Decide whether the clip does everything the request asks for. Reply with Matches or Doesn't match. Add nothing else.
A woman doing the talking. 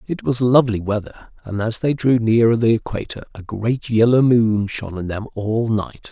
Doesn't match